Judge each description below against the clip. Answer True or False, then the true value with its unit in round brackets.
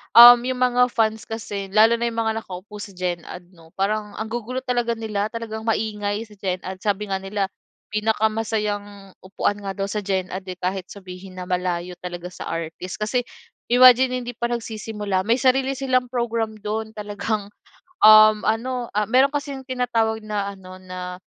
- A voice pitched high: True (215 Hz)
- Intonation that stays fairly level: False (3.3 semitones)